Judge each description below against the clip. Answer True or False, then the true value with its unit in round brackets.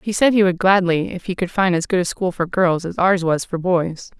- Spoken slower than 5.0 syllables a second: False (5.2 syllables/s)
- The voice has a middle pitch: True (180 Hz)